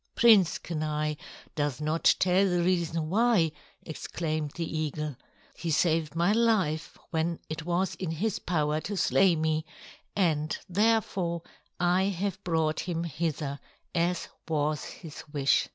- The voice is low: No, medium, 165 Hz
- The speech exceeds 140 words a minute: No, slow, 135 wpm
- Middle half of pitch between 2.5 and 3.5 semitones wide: Yes, average, 2.9 semitones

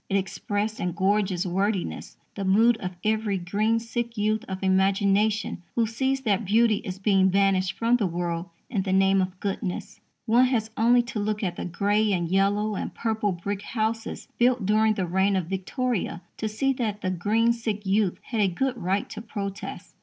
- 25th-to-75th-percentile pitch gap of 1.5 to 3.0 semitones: Yes, narrow, 2.6 semitones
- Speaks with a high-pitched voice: Yes, high, 205 Hz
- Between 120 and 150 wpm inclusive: No, average, 185 wpm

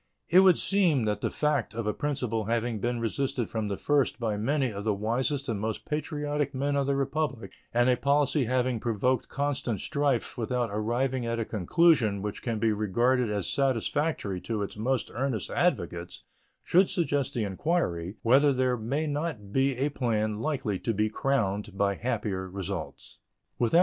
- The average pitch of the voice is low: Yes, low, 120 Hz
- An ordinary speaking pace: Yes, average, 170 wpm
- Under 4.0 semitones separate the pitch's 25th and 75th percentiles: No, average, 4.7 semitones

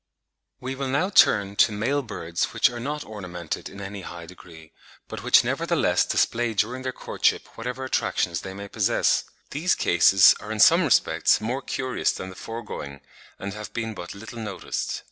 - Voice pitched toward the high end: No, low, 110 Hz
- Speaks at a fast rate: No, average, 175 wpm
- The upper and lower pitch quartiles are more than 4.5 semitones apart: Yes, average, 5.2 semitones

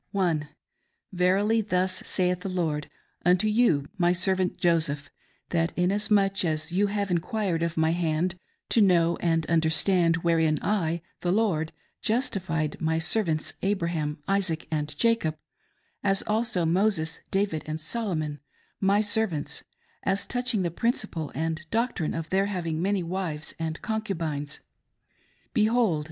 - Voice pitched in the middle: Yes, medium, 180 Hz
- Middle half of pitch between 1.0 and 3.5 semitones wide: No, average, 3.9 semitones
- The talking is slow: Yes, slow, 130 wpm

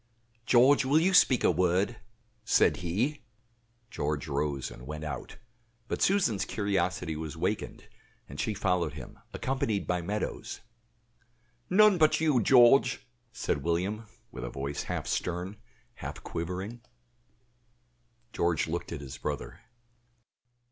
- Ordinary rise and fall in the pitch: No, wide, 7.4 semitones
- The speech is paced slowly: Yes, slow, 125 wpm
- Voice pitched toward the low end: Yes, very low, 95 Hz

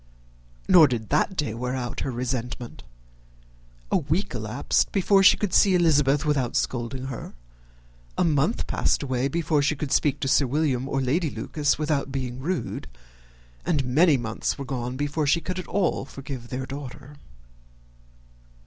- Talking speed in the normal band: Yes, average, 160 wpm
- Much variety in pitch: No, average, 3.5 semitones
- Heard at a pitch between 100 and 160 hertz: Yes, medium, 140 Hz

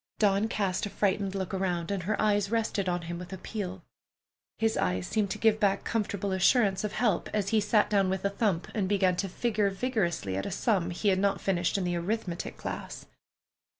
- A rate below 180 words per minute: No, fast, 205 wpm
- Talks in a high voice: Yes, high, 195 Hz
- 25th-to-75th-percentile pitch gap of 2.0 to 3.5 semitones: Yes, narrow, 2.5 semitones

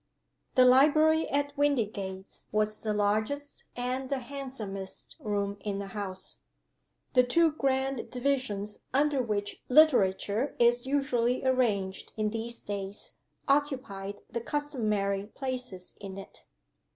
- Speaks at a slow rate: Yes, slow, 115 wpm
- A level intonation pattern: No, average, 5.1 semitones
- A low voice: No, high, 235 Hz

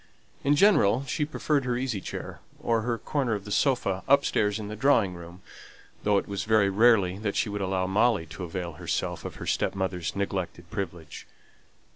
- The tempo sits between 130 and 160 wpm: No, average, 180 wpm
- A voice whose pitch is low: Yes, low, 100 Hz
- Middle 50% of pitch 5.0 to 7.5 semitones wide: No, average, 4.4 semitones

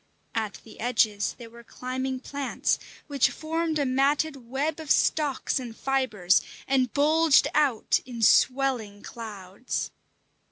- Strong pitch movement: No, average, 3.8 semitones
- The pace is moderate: No, slow, 125 wpm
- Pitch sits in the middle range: No, very high, 260 Hz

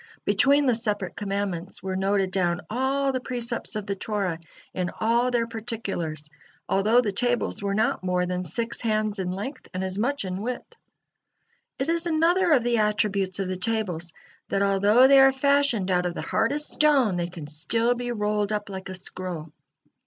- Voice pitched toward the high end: Yes, high, 210 Hz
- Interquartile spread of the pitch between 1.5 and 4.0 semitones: No, average, 4.5 semitones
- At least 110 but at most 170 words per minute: No, average, 180 wpm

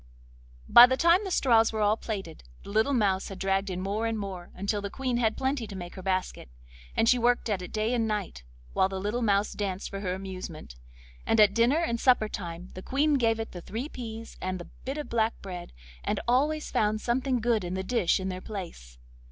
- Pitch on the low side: No, high, 215 Hz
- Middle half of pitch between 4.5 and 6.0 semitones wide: No, average, 4.1 semitones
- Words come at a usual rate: No, fast, 225 wpm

